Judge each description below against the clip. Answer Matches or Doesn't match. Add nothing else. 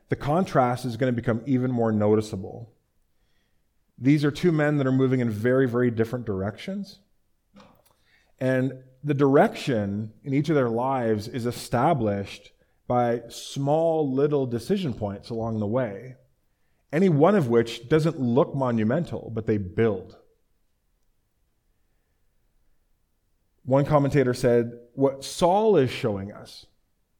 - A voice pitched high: Doesn't match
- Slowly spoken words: Matches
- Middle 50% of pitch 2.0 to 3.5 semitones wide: Doesn't match